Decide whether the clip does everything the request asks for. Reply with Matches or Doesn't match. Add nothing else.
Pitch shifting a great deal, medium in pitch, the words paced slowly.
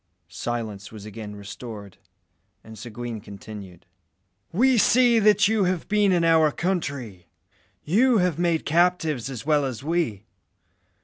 Matches